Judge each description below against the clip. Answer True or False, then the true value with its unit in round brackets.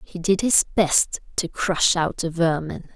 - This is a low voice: False (175 Hz)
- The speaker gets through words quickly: False (185 wpm)